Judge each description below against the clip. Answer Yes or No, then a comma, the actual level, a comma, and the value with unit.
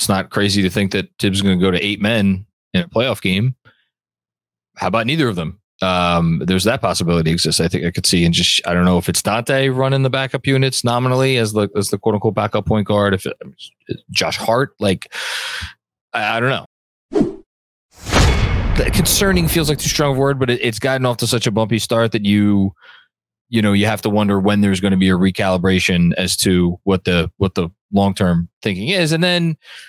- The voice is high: No, low, 100 Hz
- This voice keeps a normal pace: No, fast, 215 wpm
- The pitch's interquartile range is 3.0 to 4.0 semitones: No, average, 4.4 semitones